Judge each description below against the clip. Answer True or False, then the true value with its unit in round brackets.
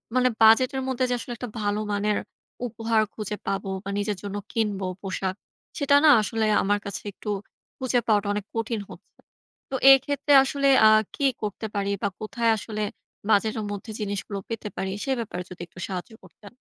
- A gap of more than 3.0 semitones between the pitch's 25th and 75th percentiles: False (2.7 semitones)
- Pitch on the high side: True (215 Hz)